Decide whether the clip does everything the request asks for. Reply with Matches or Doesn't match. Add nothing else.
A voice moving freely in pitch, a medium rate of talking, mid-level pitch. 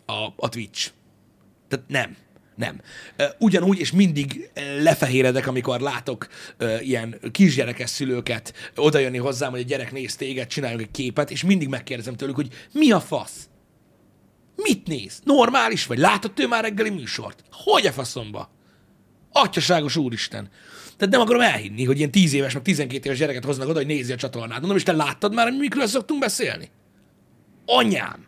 Doesn't match